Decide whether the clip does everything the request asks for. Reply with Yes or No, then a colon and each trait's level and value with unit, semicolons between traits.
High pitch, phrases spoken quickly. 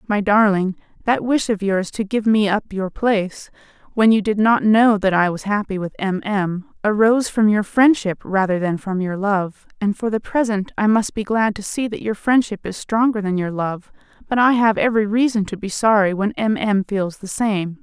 Yes: high, 205 Hz; fast, 220 wpm